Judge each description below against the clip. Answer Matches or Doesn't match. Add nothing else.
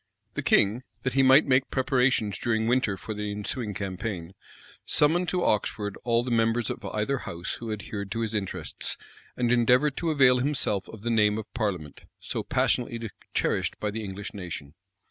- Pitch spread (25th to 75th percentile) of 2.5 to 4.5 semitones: Matches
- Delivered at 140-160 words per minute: Doesn't match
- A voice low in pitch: Matches